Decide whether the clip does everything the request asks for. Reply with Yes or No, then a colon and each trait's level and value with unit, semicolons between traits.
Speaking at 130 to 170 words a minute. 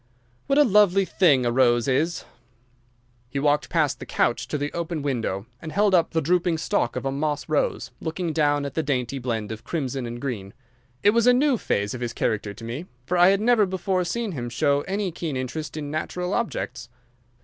No: fast, 205 wpm